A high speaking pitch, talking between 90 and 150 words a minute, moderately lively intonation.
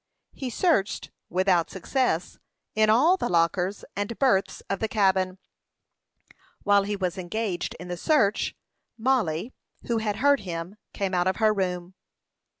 Yes: high, 200 Hz; average, 145 wpm; average, 3.6 semitones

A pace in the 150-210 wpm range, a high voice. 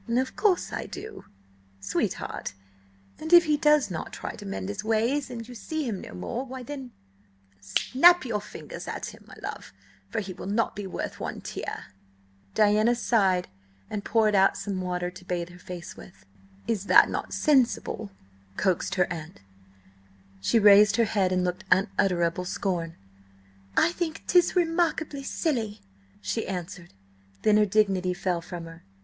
Yes: average, 160 wpm; high, 205 Hz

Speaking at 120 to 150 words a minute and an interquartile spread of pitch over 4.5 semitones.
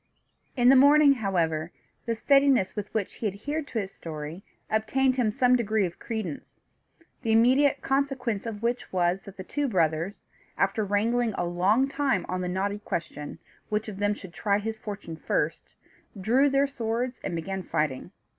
No: average, 170 wpm; average, 5.2 semitones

